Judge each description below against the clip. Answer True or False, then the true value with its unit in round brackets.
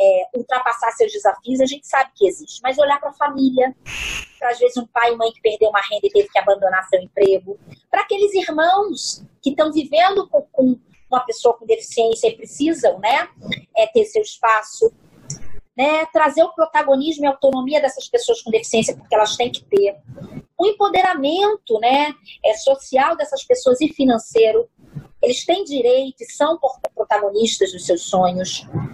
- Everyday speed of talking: True (170 wpm)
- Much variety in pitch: True (6.0 semitones)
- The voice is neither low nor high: False (260 Hz)